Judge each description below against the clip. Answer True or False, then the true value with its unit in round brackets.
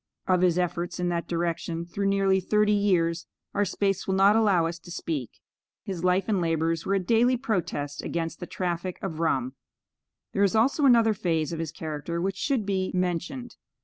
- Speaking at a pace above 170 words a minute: True (185 wpm)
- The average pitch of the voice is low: False (180 Hz)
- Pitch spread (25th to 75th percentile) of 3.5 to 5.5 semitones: False (3.1 semitones)